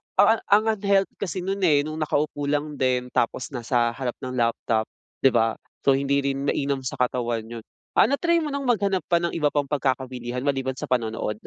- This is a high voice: No, medium, 140 Hz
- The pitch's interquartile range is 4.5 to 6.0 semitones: Yes, wide, 5.4 semitones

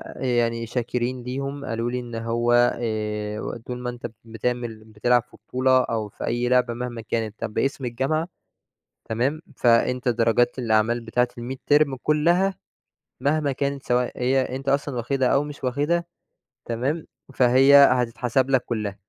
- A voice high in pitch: No, low, 125 Hz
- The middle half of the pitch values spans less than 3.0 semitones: Yes, narrow, 2.5 semitones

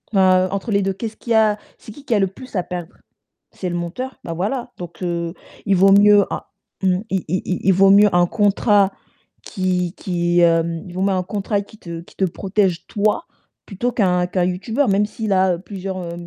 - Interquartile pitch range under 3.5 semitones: Yes, narrow, 2.5 semitones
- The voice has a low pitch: No, high, 190 Hz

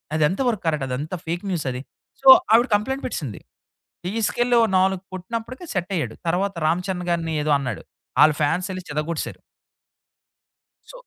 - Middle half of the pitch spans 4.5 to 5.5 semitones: Yes, average, 4.8 semitones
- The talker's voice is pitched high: No, medium, 180 Hz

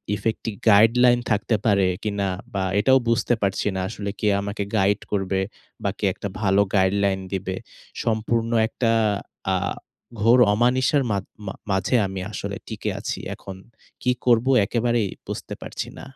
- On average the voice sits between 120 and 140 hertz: No, low, 105 Hz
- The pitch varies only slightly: No, average, 3.0 semitones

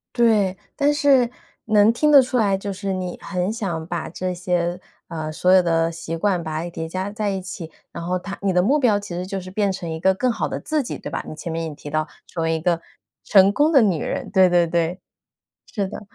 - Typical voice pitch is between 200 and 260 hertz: No, medium, 185 Hz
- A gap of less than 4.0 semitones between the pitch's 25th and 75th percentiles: Yes, average, 3.5 semitones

